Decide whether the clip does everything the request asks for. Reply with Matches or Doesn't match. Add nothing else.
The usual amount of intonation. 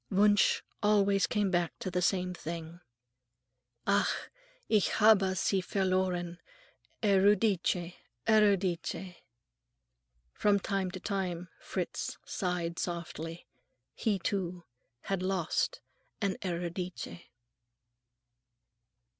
Doesn't match